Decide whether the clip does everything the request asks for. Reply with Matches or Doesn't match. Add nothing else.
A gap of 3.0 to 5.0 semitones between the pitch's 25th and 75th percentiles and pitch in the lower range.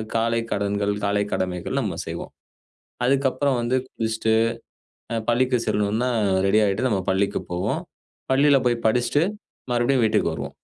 Matches